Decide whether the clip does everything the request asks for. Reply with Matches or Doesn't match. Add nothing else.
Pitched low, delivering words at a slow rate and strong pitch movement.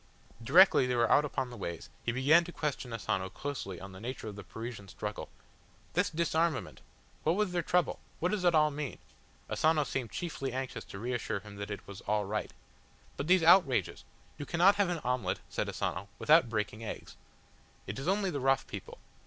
Doesn't match